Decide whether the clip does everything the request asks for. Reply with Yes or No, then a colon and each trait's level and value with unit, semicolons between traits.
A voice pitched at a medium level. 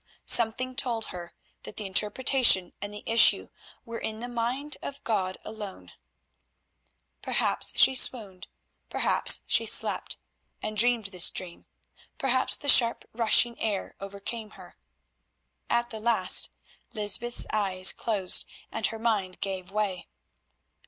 No: high, 220 Hz